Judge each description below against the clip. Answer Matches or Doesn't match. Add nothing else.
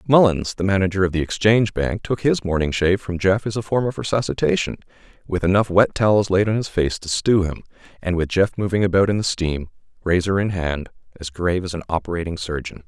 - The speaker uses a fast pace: Matches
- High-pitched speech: Doesn't match